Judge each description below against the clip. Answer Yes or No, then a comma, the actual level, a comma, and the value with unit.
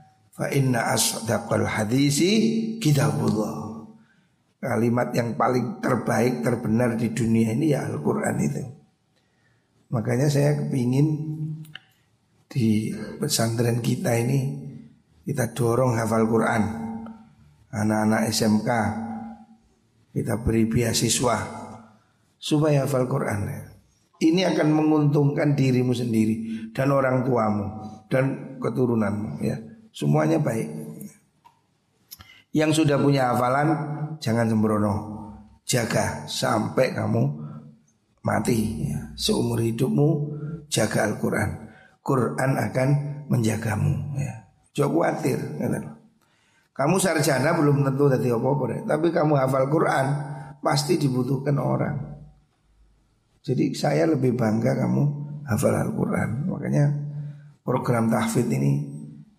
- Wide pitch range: No, average, 4.7 semitones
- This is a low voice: Yes, low, 125 Hz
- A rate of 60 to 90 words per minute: Yes, slow, 85 wpm